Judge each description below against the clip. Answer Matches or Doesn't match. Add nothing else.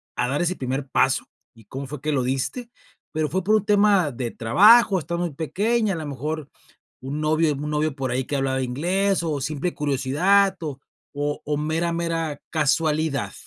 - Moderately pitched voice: Matches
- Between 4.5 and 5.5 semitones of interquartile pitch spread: Doesn't match